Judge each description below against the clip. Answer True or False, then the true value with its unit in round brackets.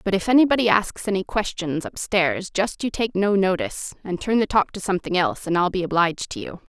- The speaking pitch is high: True (195 Hz)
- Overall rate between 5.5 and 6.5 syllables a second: True (5.9 syllables/s)